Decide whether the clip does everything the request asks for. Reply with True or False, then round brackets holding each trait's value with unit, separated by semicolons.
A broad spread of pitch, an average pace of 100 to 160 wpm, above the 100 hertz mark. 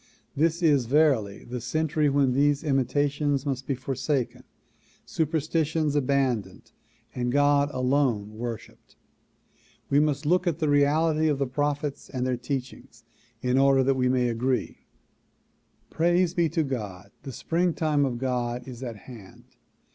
False (3.1 semitones; 140 wpm; 140 Hz)